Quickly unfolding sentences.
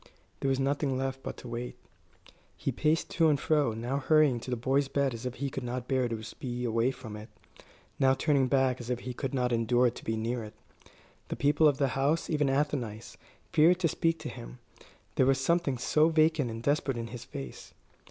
Yes: fast, 210 wpm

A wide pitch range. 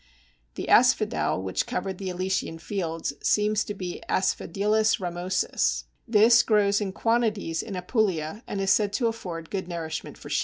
No: average, 3.4 semitones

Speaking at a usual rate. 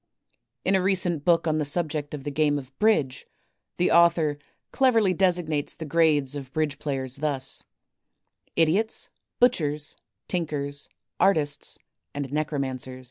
No: slow, 130 wpm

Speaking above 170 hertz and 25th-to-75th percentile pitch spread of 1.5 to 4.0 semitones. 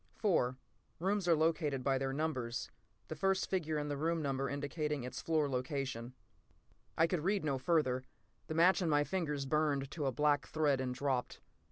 No: medium, 150 Hz; average, 3.3 semitones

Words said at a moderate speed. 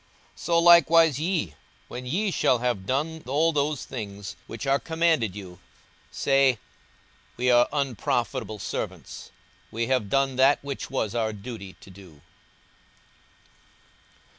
No: slow, 130 wpm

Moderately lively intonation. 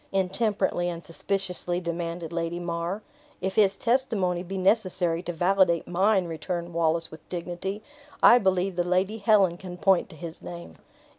No: narrow, 2.3 semitones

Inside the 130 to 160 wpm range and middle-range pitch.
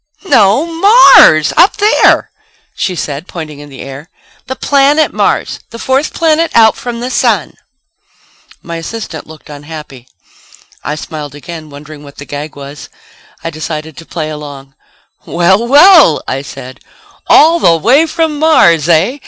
Yes: average, 150 wpm; medium, 165 Hz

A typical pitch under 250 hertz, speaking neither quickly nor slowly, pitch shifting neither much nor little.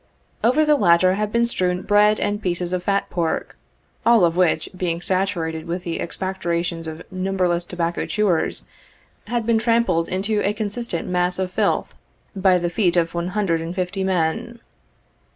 Yes: medium, 185 Hz; average, 165 wpm; average, 3.2 semitones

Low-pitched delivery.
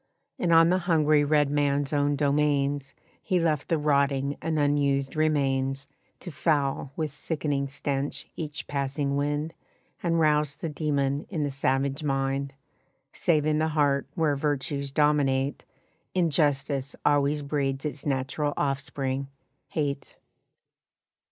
No: medium, 145 Hz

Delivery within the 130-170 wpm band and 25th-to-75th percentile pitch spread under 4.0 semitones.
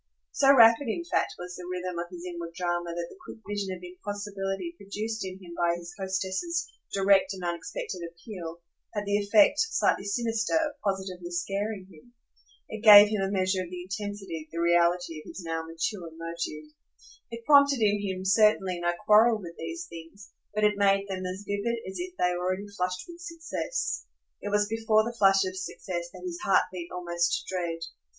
No: average, 185 wpm; average, 3.2 semitones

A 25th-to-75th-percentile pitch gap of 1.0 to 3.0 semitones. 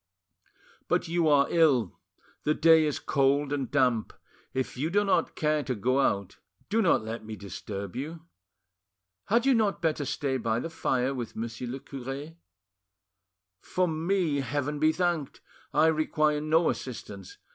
No: average, 4.3 semitones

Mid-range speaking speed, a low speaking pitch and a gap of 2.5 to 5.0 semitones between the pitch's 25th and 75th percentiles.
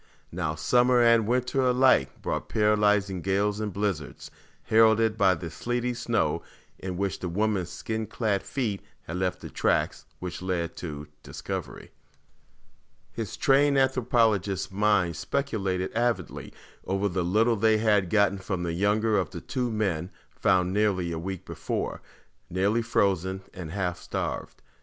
Yes: average, 145 wpm; low, 100 Hz; average, 3.5 semitones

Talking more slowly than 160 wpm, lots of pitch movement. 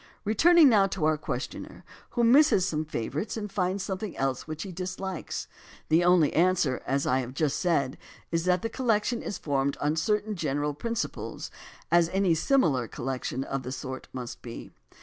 No: average, 175 wpm; wide, 6.2 semitones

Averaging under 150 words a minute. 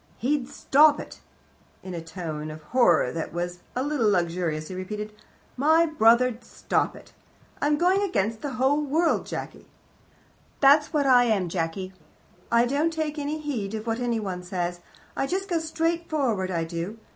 No: average, 165 wpm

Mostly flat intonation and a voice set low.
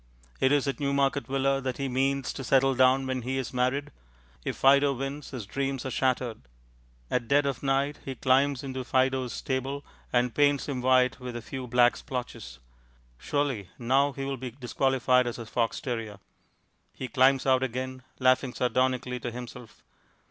Yes: narrow, 1.6 semitones; low, 130 Hz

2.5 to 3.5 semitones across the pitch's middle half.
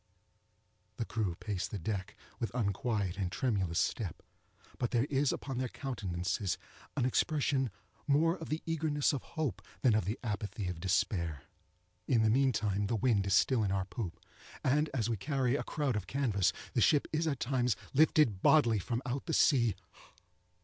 No: wide, 5.5 semitones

